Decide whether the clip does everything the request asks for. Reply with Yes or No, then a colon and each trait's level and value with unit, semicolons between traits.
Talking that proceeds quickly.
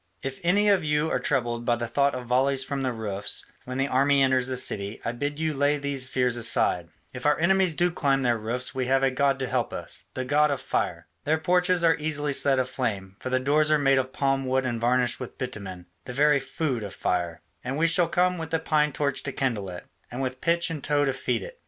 Yes: fast, 240 wpm